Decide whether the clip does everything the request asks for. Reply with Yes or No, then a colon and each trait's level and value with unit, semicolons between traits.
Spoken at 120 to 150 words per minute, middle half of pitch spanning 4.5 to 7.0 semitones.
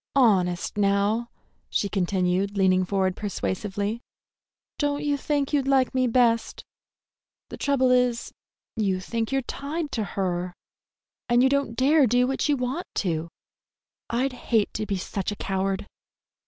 Yes: average, 140 wpm; average, 5.2 semitones